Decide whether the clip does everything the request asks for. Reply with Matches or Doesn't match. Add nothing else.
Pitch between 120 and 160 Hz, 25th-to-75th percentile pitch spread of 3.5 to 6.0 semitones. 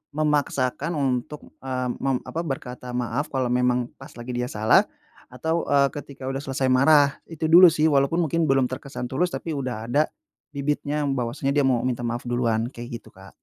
Doesn't match